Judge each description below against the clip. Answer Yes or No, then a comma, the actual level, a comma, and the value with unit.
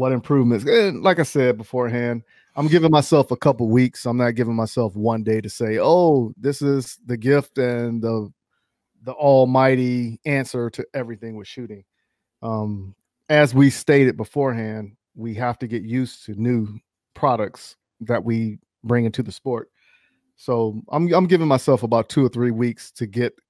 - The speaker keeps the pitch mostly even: No, average, 3.1 semitones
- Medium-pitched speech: No, low, 120 Hz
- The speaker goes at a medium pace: Yes, average, 170 wpm